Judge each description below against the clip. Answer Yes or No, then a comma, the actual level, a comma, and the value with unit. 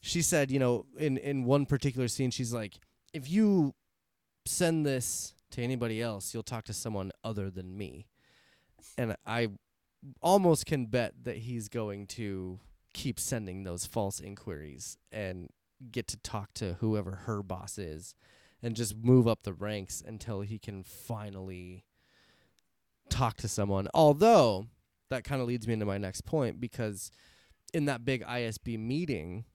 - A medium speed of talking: Yes, average, 155 wpm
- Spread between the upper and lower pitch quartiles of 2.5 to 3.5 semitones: No, average, 4.4 semitones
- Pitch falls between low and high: No, low, 110 Hz